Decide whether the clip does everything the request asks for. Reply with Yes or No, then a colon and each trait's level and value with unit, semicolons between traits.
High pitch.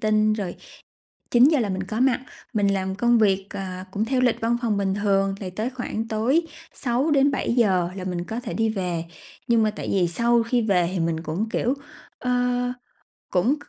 Yes: high, 215 Hz